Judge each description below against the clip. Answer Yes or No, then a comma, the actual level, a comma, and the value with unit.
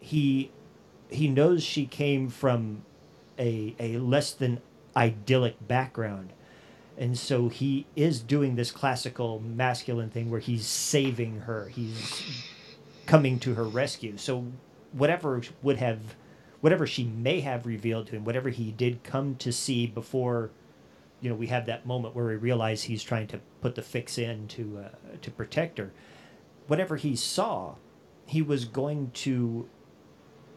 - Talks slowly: No, average, 150 wpm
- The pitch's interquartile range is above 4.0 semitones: No, average, 3.2 semitones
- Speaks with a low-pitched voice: Yes, low, 120 Hz